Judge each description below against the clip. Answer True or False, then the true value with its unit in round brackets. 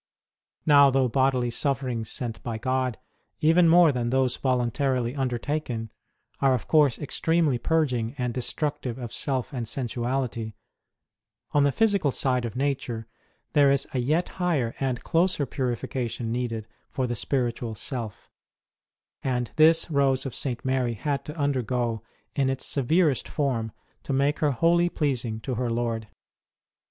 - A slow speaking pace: False (145 wpm)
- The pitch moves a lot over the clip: False (3.1 semitones)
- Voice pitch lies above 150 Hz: False (130 Hz)